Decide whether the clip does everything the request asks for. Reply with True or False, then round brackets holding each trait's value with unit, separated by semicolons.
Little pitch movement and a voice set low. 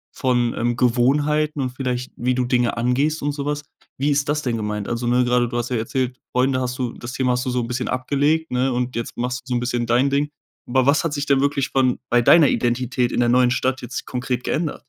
True (2.2 semitones; 125 Hz)